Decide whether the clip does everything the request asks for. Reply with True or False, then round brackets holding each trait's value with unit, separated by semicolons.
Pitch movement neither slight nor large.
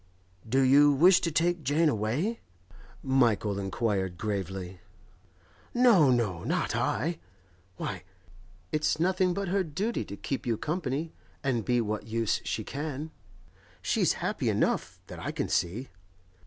False (7.5 semitones)